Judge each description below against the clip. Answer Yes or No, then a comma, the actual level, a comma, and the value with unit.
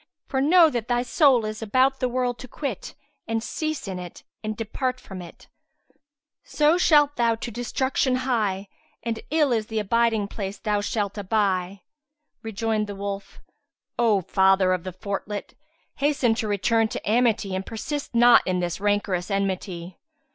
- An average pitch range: Yes, average, 4.1 semitones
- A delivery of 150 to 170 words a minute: Yes, average, 160 wpm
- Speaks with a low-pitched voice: No, high, 220 Hz